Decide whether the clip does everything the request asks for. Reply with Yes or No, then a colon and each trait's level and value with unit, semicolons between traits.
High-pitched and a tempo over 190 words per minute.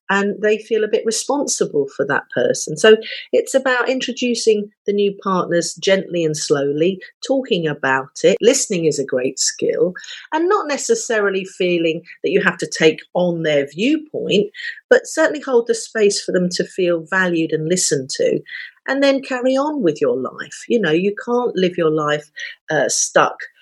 No: high, 220 Hz; average, 175 wpm